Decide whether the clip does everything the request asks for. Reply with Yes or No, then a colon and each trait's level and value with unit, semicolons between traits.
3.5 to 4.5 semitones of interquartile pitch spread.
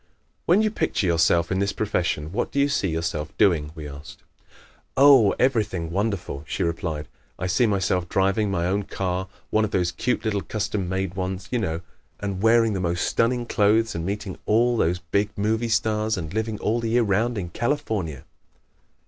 Yes: average, 4.2 semitones